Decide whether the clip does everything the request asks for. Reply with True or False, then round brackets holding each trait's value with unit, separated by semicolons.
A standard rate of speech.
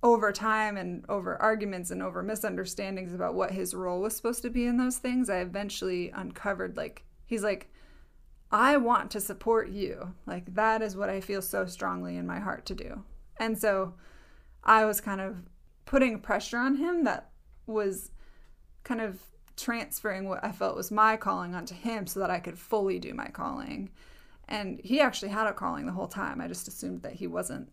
True (195 wpm)